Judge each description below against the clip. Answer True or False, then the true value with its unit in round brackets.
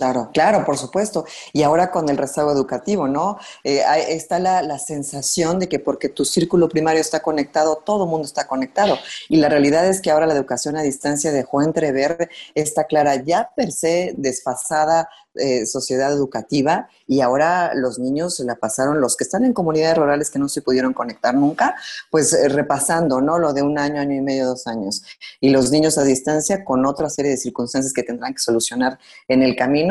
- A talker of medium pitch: True (145 Hz)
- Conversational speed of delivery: False (195 wpm)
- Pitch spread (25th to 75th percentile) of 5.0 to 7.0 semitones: False (3.1 semitones)